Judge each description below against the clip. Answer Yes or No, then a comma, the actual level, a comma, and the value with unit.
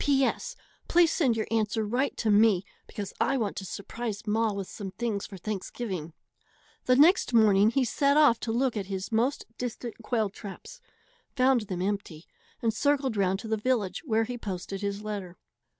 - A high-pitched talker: Yes, high, 220 Hz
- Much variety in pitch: No, average, 3.9 semitones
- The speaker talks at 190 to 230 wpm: No, average, 180 wpm